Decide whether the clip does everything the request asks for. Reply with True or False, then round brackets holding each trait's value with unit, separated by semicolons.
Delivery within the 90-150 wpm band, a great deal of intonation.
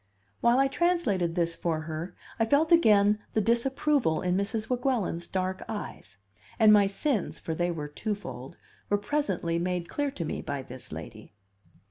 False (160 wpm; 6.0 semitones)